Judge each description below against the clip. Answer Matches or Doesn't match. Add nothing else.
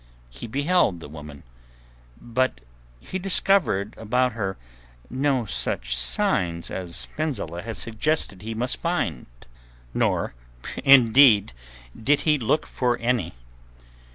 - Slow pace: Matches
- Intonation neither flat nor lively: Doesn't match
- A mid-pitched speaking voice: Doesn't match